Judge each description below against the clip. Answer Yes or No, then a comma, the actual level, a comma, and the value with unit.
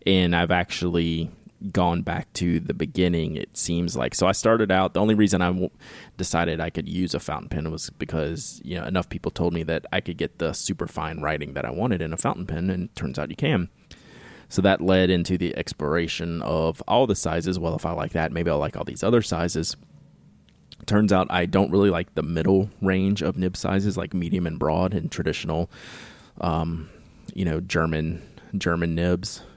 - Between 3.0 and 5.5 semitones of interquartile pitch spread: No, narrow, 2.5 semitones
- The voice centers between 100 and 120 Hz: No, very low, 85 Hz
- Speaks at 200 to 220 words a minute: Yes, fast, 205 wpm